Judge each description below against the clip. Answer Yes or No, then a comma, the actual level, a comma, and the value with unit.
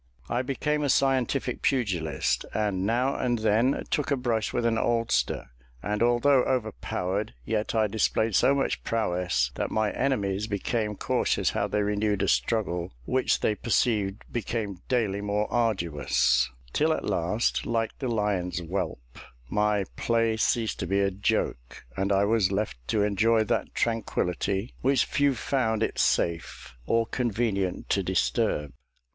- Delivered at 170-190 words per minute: No, average, 150 wpm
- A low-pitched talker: Yes, low, 110 Hz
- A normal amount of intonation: Yes, average, 3.4 semitones